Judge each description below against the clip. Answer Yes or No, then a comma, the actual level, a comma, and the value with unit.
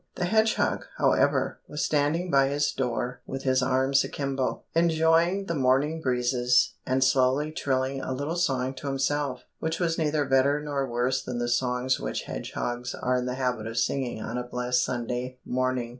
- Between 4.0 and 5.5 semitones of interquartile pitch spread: No, average, 2.8 semitones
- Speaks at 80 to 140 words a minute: No, average, 175 wpm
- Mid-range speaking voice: No, low, 130 Hz